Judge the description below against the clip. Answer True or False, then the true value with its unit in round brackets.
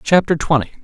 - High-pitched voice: False (155 Hz)